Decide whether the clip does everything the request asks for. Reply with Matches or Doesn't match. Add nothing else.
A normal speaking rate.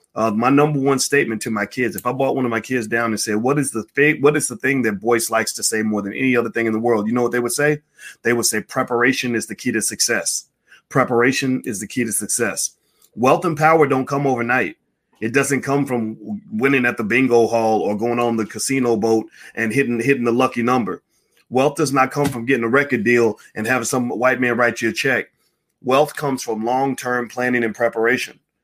Doesn't match